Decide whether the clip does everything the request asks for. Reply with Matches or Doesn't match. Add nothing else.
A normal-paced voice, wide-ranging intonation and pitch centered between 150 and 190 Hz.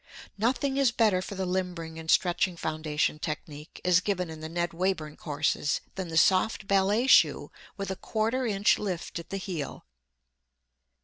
Doesn't match